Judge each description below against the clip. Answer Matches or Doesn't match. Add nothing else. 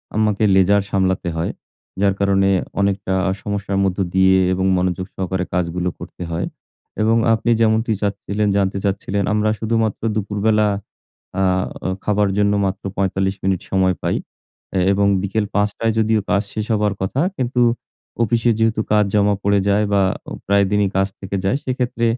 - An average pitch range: Doesn't match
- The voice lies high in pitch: Doesn't match